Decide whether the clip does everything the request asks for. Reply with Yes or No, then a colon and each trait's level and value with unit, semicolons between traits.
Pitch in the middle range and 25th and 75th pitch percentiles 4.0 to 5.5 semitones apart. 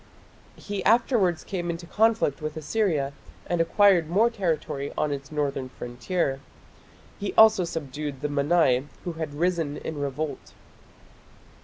Yes: medium, 160 Hz; average, 4.5 semitones